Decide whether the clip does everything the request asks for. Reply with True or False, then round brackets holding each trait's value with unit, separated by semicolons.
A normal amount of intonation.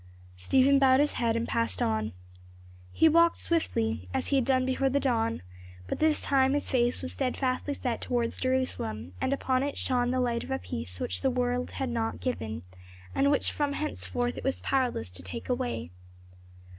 True (3.3 semitones)